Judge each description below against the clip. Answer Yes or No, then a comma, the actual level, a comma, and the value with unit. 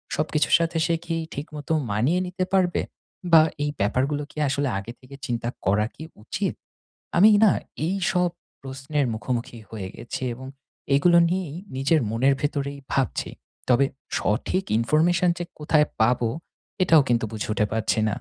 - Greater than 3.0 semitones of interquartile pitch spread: Yes, wide, 5.6 semitones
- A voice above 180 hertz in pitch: No, medium, 140 Hz